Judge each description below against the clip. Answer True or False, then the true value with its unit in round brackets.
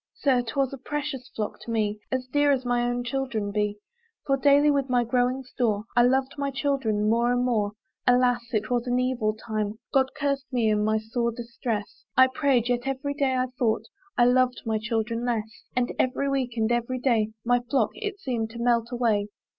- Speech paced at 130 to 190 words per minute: False (200 wpm)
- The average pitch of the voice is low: False (245 Hz)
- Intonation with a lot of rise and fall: False (2.8 semitones)